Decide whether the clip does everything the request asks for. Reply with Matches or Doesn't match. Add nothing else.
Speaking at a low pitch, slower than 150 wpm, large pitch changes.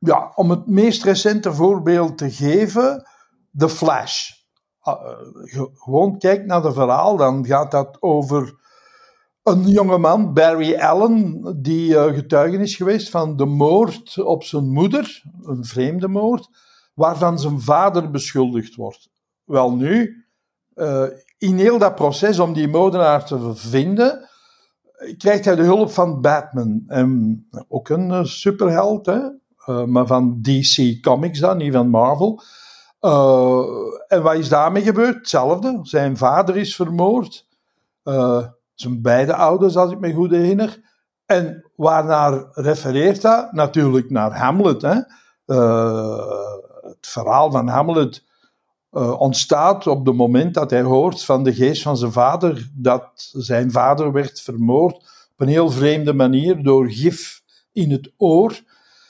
Doesn't match